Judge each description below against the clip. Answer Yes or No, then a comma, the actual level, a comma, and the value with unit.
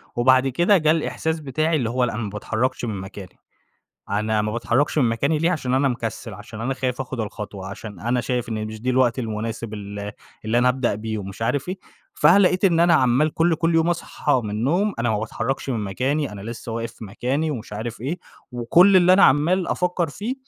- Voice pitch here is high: No, low, 125 Hz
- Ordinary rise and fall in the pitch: No, wide, 5.9 semitones